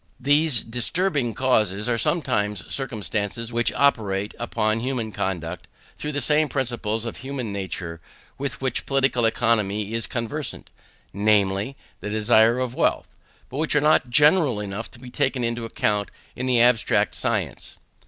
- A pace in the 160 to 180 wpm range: No, average, 145 wpm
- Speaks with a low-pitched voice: Yes, low, 115 Hz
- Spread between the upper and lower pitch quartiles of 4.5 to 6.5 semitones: No, average, 4.0 semitones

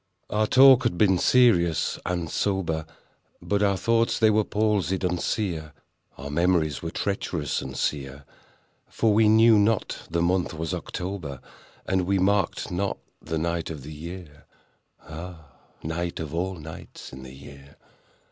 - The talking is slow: No, average, 150 wpm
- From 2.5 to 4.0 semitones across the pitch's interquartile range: No, average, 4.4 semitones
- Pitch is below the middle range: Yes, very low, 90 Hz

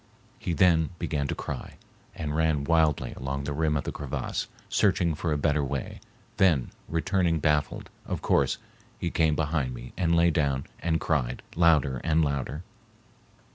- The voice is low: Yes, very low, 75 Hz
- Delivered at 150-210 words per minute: Yes, average, 160 wpm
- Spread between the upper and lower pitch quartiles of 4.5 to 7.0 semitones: No, average, 2.7 semitones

